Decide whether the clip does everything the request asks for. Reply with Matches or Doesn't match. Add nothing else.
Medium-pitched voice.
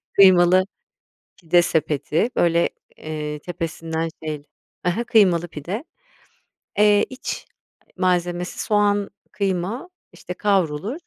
Matches